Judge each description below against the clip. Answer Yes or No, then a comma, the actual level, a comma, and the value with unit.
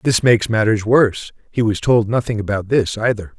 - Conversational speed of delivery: Yes, average, 195 wpm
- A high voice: No, low, 110 Hz